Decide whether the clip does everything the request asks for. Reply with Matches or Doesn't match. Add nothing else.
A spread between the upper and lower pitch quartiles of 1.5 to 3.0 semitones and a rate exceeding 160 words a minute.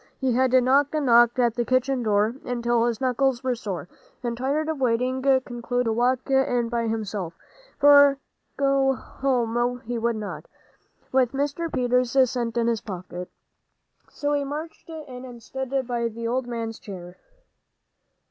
Doesn't match